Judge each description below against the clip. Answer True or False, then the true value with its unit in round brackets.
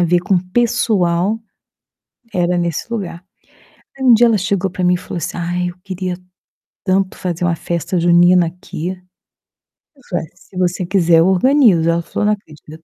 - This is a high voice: False (180 Hz)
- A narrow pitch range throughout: True (2.1 semitones)